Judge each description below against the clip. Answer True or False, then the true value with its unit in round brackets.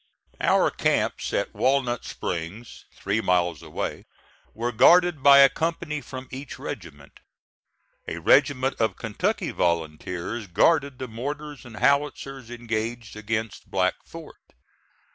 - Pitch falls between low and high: False (120 Hz)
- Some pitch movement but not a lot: True (4.9 semitones)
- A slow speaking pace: True (120 wpm)